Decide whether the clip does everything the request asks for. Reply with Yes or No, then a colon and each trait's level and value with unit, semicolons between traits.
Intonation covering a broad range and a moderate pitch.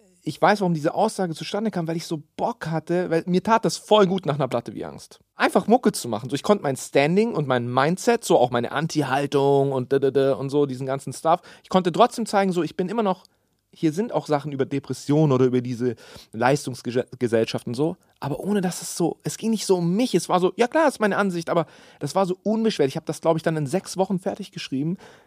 Yes: wide, 5.8 semitones; medium, 165 Hz